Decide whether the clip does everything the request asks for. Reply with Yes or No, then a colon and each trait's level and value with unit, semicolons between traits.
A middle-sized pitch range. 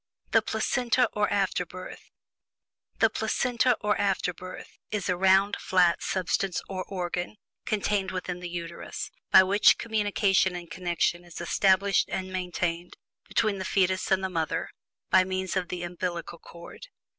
No: narrow, 2.1 semitones